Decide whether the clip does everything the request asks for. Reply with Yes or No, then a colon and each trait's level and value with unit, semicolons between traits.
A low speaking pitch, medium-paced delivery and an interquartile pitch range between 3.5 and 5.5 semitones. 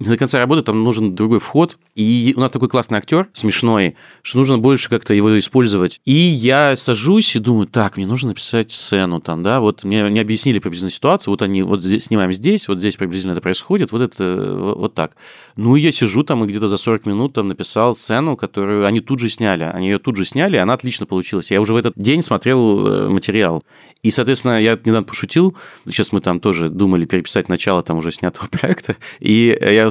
No: low, 110 Hz; fast, 210 wpm; average, 4.5 semitones